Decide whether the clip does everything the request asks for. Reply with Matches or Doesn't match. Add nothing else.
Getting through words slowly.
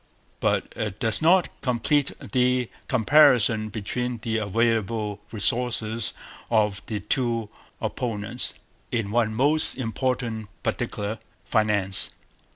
Matches